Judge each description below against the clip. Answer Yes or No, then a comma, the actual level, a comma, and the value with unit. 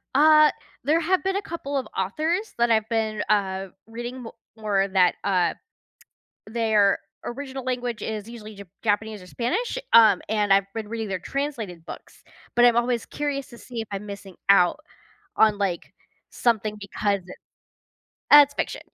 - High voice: Yes, high, 225 Hz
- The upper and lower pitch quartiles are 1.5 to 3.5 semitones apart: No, average, 4.5 semitones